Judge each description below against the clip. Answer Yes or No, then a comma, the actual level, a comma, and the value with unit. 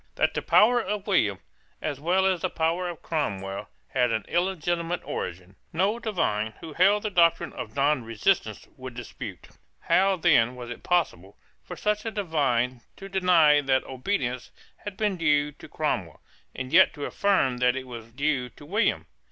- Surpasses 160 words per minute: Yes, average, 170 wpm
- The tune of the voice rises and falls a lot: Yes, wide, 7.2 semitones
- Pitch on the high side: No, medium, 155 Hz